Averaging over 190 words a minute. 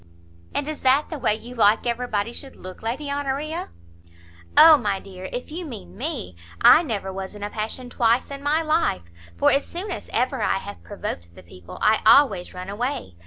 Yes: average, 200 wpm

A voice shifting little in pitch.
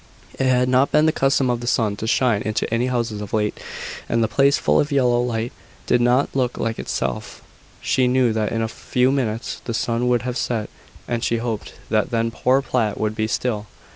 Yes: narrow, 2.3 semitones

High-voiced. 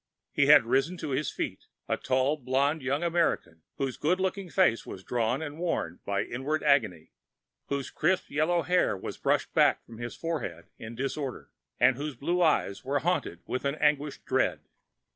No: medium, 140 Hz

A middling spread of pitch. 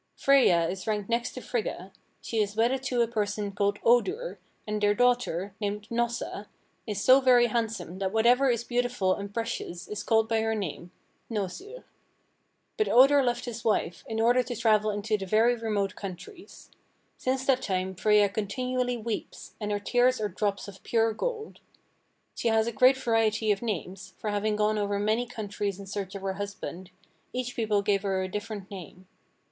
Yes: average, 3.1 semitones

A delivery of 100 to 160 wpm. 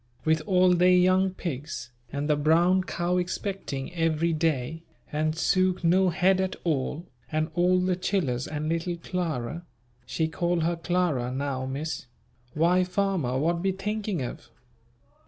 Yes: average, 145 wpm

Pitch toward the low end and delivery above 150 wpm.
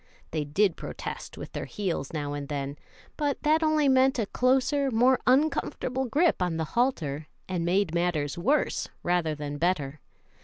No: medium, 185 Hz; average, 160 wpm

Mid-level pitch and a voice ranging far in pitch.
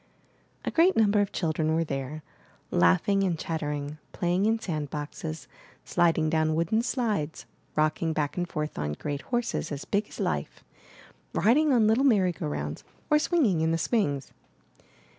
Yes: medium, 165 Hz; wide, 5.8 semitones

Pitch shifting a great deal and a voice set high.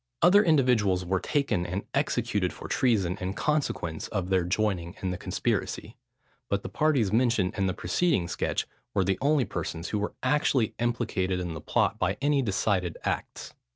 No: wide, 5.7 semitones; low, 100 Hz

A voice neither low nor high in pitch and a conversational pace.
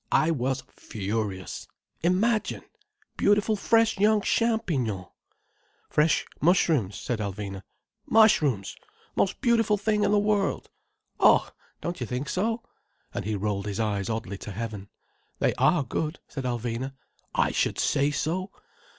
No: medium, 145 Hz; slow, 125 wpm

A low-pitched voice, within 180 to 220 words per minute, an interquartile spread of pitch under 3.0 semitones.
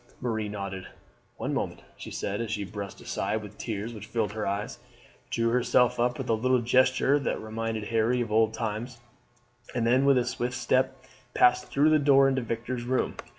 Yes: low, 115 Hz; average, 190 wpm; narrow, 2.6 semitones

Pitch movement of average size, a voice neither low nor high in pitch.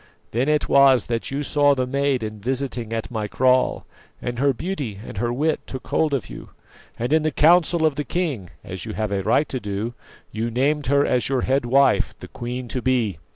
No: average, 3.6 semitones; low, 130 Hz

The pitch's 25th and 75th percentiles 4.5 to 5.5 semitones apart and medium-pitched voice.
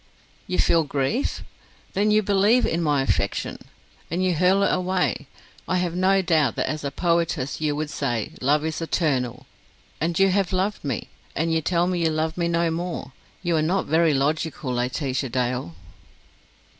No: average, 4.1 semitones; medium, 165 Hz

